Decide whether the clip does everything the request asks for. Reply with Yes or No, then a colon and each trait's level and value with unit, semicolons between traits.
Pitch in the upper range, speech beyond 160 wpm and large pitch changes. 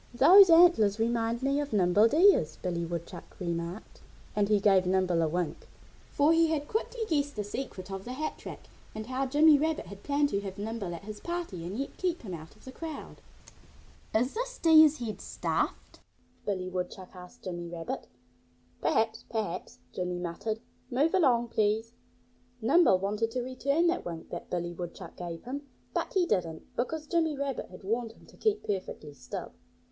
Yes: high, 220 Hz; average, 175 wpm; wide, 7.9 semitones